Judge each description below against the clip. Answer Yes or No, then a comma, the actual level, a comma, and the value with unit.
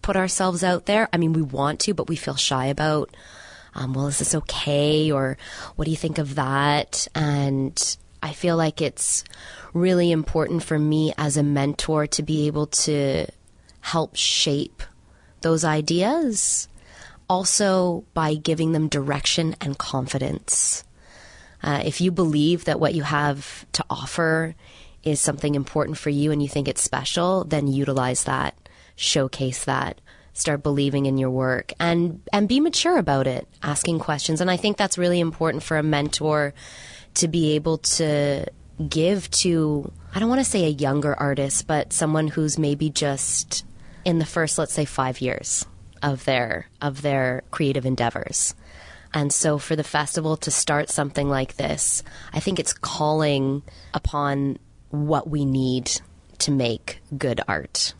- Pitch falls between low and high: Yes, medium, 150 Hz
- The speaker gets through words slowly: No, average, 160 wpm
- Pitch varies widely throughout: No, average, 2.7 semitones